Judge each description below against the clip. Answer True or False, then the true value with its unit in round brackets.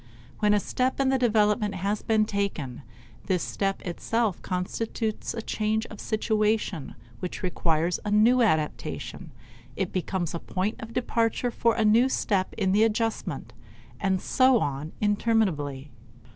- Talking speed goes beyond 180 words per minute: False (145 wpm)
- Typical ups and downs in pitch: True (3.6 semitones)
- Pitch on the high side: True (210 Hz)